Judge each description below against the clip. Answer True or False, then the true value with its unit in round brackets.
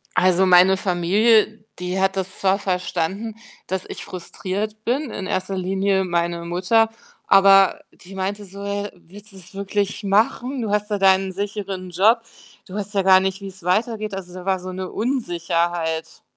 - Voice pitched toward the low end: False (195 Hz)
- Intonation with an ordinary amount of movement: False (2.1 semitones)